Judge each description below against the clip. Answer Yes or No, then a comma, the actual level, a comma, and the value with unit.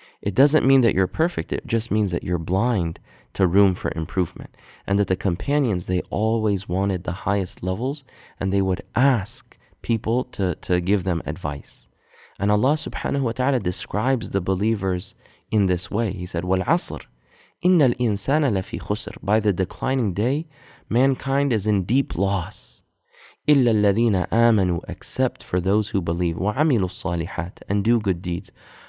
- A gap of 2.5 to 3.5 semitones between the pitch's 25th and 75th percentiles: No, average, 4.7 semitones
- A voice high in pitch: No, low, 100 Hz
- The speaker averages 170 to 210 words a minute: No, average, 155 wpm